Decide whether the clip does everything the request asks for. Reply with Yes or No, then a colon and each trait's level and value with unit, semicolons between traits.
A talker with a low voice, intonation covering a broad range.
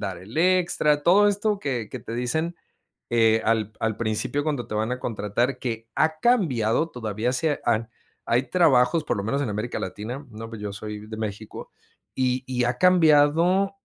Yes: low, 125 Hz; wide, 5.9 semitones